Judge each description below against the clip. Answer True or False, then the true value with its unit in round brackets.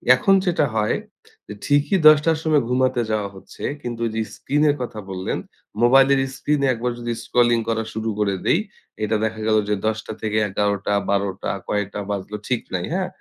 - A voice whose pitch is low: True (115 Hz)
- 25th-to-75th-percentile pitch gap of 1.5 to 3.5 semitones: False (4.7 semitones)